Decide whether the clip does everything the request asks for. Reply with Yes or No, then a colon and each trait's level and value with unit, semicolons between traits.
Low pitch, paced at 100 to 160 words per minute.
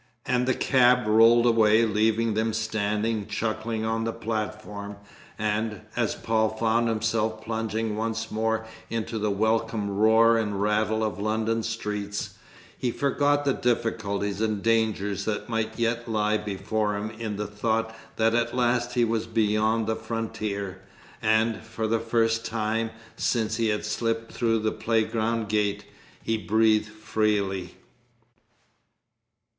Yes: low, 110 Hz; average, 140 wpm